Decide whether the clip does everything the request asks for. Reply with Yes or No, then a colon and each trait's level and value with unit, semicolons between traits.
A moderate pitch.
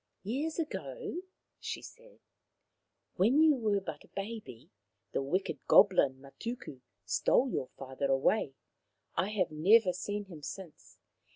No: high, 195 Hz